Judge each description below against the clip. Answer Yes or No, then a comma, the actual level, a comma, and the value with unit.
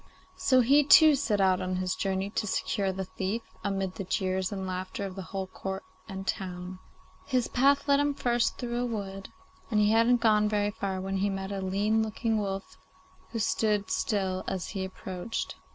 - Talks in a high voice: Yes, high, 200 Hz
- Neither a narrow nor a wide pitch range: Yes, average, 3.2 semitones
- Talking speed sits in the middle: Yes, average, 190 wpm